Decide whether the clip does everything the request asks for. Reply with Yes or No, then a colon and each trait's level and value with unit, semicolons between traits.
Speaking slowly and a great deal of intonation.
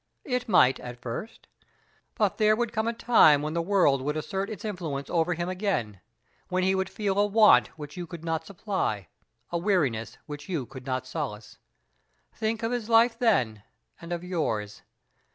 No: average, 180 wpm; wide, 7.3 semitones